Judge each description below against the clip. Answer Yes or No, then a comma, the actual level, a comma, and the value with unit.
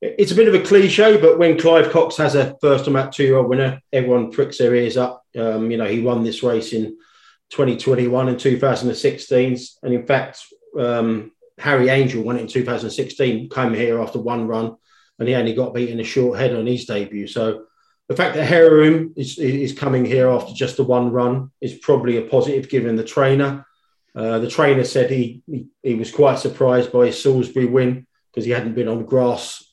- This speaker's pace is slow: No, average, 200 wpm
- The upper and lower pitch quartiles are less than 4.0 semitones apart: Yes, narrow, 2.4 semitones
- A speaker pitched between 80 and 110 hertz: No, low, 125 Hz